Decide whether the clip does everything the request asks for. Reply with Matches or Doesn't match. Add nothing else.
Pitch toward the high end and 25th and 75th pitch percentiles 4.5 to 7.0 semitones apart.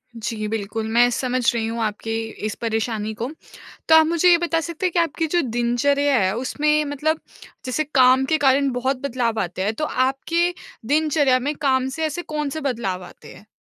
Matches